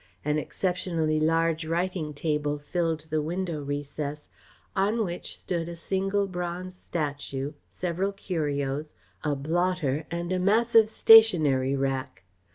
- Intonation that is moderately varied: Yes, average, 3.7 semitones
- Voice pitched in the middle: Yes, medium, 165 Hz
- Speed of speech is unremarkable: No, slow, 120 wpm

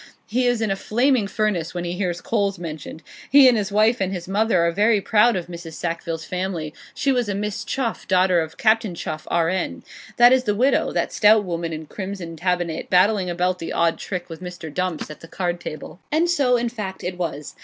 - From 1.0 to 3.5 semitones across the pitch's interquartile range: No, average, 4.2 semitones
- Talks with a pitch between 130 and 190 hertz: Yes, medium, 185 Hz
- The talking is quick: Yes, fast, 220 wpm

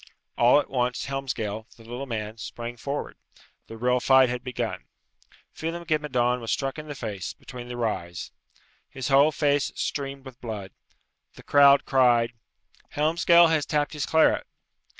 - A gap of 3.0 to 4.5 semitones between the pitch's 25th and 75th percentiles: Yes, average, 3.4 semitones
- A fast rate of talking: No, average, 155 wpm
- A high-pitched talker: No, low, 130 Hz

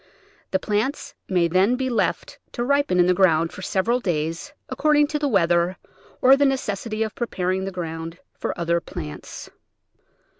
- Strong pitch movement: Yes, wide, 6.6 semitones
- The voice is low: No, high, 190 Hz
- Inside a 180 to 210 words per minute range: No, average, 165 wpm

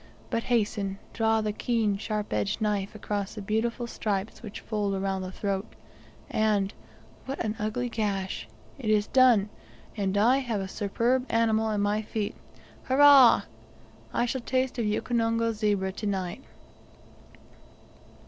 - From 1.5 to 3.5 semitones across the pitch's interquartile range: Yes, narrow, 2.5 semitones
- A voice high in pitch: Yes, high, 215 Hz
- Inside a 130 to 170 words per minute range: Yes, average, 140 wpm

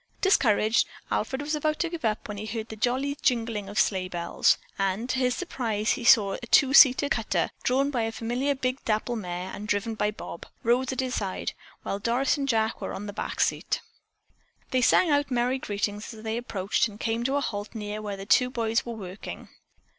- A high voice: Yes, high, 230 Hz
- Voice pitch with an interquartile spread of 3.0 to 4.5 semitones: Yes, average, 3.8 semitones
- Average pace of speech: No, fast, 210 wpm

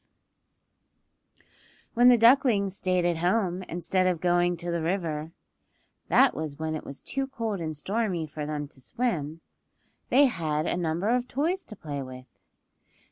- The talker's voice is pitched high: No, medium, 175 Hz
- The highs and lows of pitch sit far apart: Yes, wide, 6.1 semitones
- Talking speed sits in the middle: Yes, average, 160 wpm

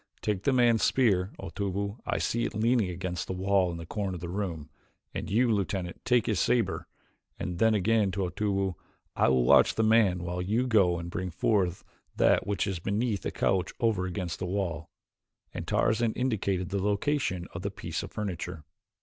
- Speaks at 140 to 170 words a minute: No, average, 190 wpm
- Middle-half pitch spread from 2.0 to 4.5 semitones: Yes, average, 3.4 semitones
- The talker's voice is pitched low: Yes, very low, 95 Hz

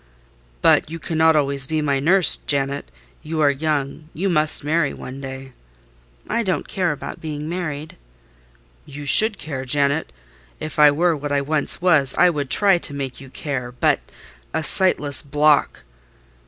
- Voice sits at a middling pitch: Yes, medium, 150 Hz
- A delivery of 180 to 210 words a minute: No, average, 150 wpm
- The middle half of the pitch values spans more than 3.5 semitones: No, narrow, 2.5 semitones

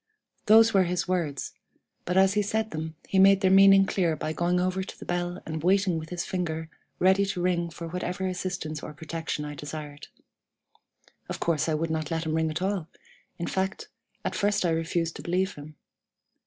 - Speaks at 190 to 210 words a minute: Yes, average, 195 wpm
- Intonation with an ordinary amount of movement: Yes, average, 3.0 semitones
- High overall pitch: No, medium, 175 Hz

